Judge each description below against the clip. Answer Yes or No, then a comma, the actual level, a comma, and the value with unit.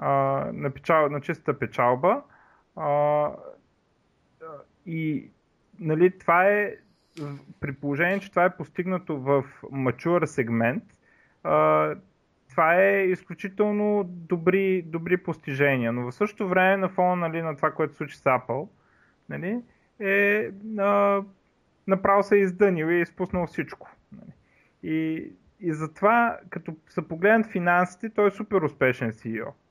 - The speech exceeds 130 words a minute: No, average, 125 wpm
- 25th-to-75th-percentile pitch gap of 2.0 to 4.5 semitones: No, average, 4.9 semitones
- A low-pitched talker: No, medium, 175 Hz